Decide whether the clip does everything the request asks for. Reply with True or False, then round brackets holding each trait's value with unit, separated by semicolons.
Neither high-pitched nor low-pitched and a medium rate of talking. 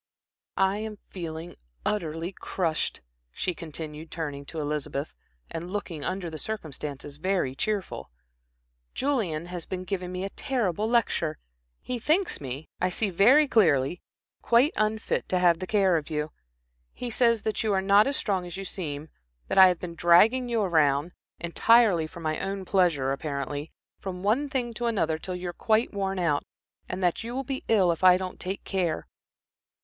True (180 Hz; 175 wpm)